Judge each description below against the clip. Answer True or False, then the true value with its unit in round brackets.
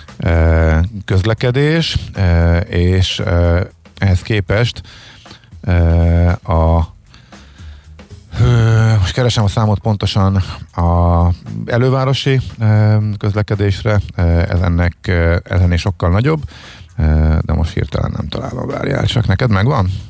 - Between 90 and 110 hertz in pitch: True (100 Hz)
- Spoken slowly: True (80 wpm)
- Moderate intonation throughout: True (4.5 semitones)